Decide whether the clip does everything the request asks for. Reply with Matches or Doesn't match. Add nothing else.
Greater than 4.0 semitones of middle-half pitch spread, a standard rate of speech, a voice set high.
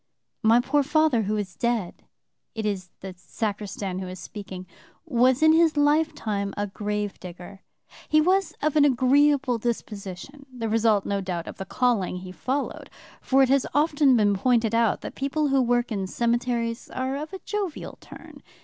Matches